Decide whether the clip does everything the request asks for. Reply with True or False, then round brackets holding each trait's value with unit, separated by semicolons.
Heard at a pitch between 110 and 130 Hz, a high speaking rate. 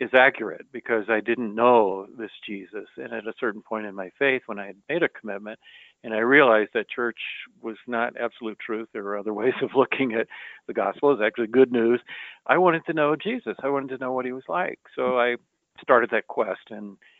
True (120 Hz; 220 wpm)